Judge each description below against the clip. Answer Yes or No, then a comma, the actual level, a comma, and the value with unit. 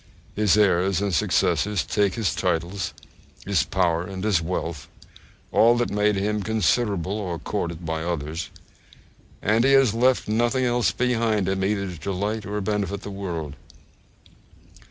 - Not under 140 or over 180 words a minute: Yes, average, 145 wpm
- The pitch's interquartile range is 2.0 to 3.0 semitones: No, average, 3.6 semitones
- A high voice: No, low, 100 Hz